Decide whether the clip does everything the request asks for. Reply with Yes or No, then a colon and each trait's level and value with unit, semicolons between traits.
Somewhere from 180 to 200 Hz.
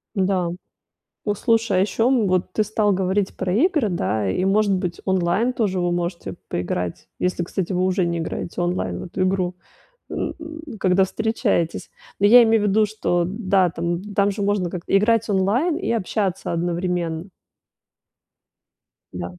Yes: high, 190 Hz